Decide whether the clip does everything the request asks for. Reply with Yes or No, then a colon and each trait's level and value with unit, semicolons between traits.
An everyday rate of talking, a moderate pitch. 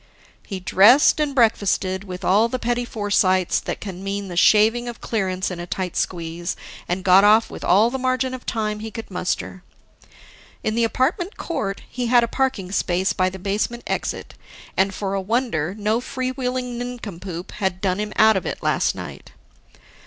No: average, 180 wpm; high, 210 Hz